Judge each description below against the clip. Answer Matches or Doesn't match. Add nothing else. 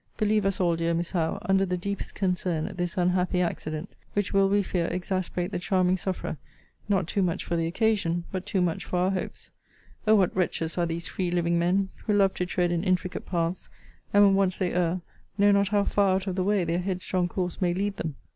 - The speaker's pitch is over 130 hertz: Matches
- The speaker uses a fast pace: Matches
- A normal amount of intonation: Doesn't match